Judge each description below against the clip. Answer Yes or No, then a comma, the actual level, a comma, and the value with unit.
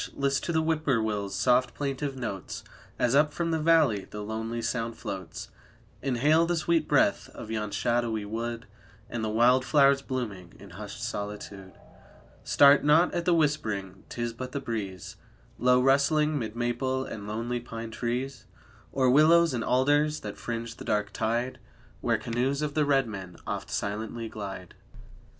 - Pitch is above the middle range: No, low, 120 Hz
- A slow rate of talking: No, average, 165 wpm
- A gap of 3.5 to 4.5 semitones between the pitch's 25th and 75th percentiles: Yes, average, 4.2 semitones